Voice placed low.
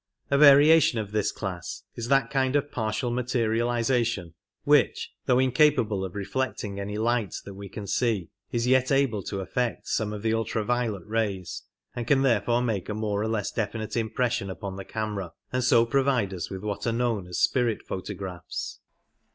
Yes: low, 115 Hz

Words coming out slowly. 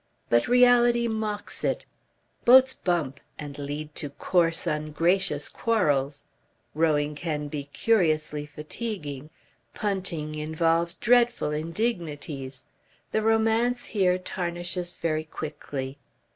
Yes: slow, 100 wpm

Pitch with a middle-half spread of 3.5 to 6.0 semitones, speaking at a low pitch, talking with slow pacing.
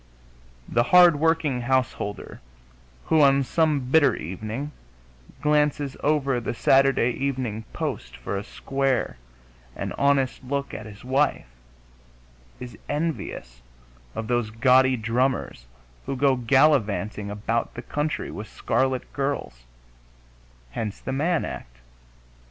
Yes: average, 4.1 semitones; low, 130 Hz; slow, 115 wpm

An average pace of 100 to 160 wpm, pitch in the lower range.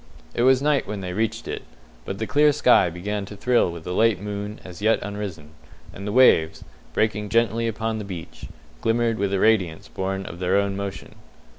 No: average, 195 wpm; low, 105 Hz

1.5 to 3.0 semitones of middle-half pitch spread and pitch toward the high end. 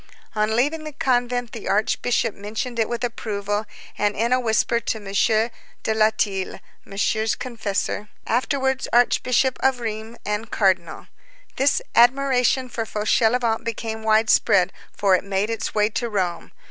Yes: average, 2.7 semitones; high, 225 Hz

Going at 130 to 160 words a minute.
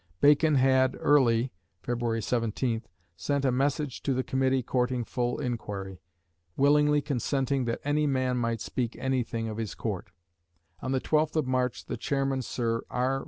Yes: average, 155 wpm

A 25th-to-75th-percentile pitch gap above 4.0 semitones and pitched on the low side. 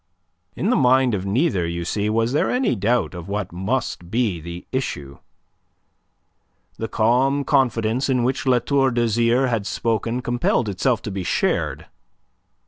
Yes: average, 4.6 semitones; low, 115 Hz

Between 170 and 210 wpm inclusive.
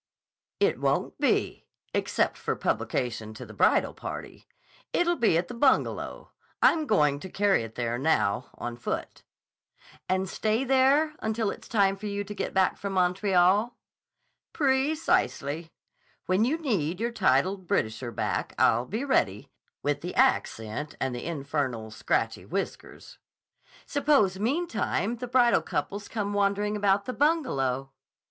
No: average, 140 wpm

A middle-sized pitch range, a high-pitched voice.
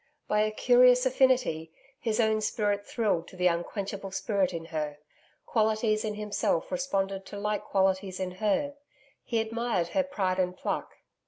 Yes: average, 3.4 semitones; high, 210 Hz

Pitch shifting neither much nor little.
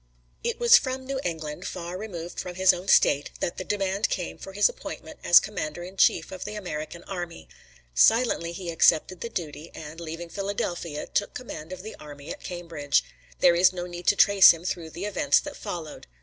Yes: average, 3.2 semitones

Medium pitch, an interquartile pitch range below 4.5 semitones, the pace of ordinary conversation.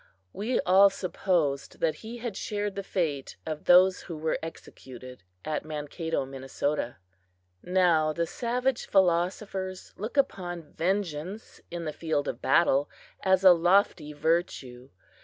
No: medium, 175 Hz; average, 4.1 semitones; slow, 130 wpm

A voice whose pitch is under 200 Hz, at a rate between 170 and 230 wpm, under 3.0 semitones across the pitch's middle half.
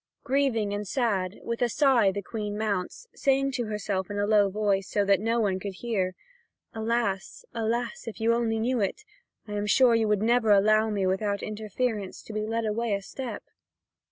No: high, 215 Hz; average, 190 wpm; narrow, 2.5 semitones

